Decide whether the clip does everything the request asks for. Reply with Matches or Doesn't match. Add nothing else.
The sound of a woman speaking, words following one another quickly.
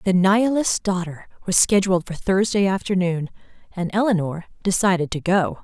Doesn't match